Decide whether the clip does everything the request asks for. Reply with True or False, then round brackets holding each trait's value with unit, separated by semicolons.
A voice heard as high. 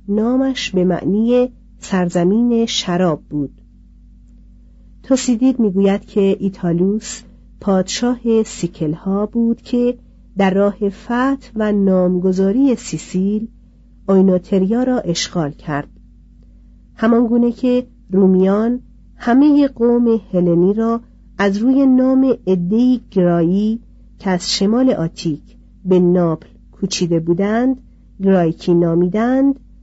True (200 Hz)